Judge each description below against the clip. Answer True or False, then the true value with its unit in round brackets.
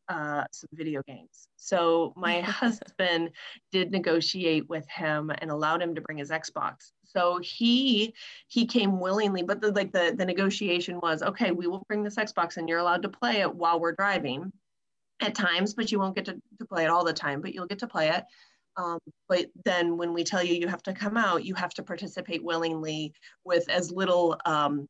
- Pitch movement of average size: True (3.0 semitones)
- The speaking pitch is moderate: True (175 Hz)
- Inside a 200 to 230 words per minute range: True (205 wpm)